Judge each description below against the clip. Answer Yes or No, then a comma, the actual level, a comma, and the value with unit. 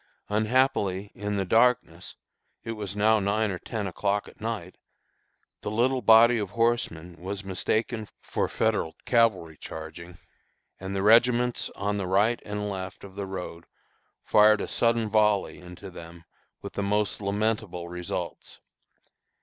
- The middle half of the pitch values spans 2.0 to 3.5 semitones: Yes, average, 2.9 semitones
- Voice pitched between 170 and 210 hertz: No, low, 105 Hz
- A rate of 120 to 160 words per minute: Yes, average, 140 wpm